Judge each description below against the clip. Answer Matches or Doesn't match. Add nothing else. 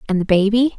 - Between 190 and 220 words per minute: Doesn't match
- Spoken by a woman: Matches